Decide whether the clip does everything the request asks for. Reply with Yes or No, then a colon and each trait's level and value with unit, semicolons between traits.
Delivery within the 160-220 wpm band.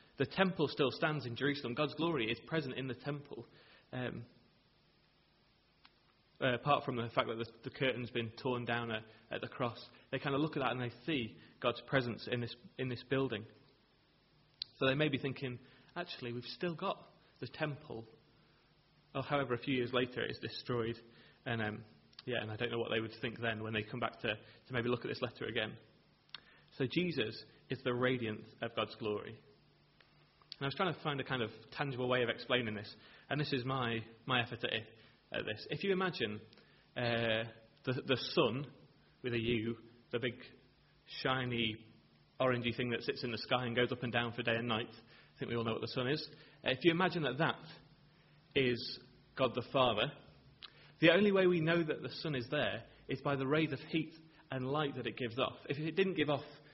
Yes: fast, 205 wpm